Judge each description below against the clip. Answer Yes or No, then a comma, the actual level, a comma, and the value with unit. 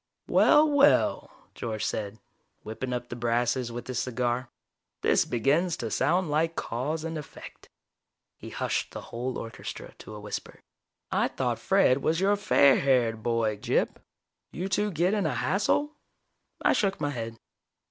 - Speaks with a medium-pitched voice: No, low, 130 Hz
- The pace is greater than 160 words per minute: No, average, 155 wpm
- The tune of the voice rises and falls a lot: Yes, wide, 6.3 semitones